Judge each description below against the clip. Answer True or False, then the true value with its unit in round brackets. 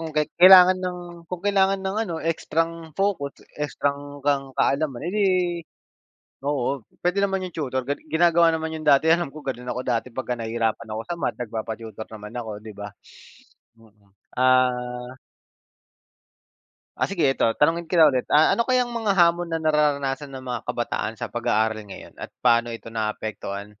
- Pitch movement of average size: False (5.9 semitones)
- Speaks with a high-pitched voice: False (145 Hz)